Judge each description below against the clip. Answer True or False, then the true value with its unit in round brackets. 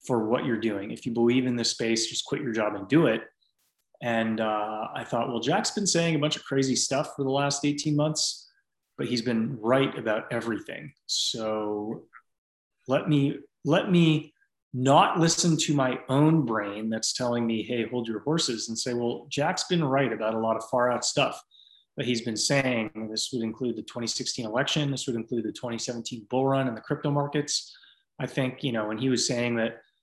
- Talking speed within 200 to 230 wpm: True (205 wpm)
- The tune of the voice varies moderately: True (4.1 semitones)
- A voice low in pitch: True (125 Hz)